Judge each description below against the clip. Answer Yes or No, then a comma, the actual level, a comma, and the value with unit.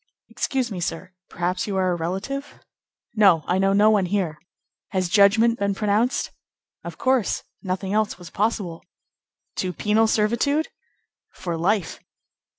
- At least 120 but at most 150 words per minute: Yes, average, 140 wpm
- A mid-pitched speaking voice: No, high, 200 Hz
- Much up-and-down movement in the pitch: No, average, 3.2 semitones